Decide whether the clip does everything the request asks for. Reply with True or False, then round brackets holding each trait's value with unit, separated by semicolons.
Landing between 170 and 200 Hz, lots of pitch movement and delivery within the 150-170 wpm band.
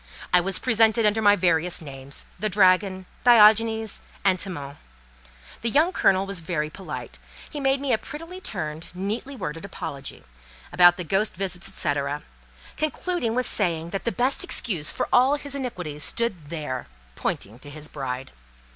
True (190 Hz; 6.5 semitones; 155 wpm)